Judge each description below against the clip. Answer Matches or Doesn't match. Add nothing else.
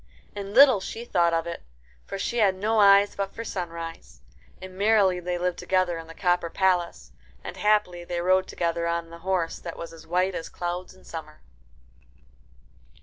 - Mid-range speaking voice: Matches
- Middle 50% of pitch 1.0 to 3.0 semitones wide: Matches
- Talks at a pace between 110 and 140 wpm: Doesn't match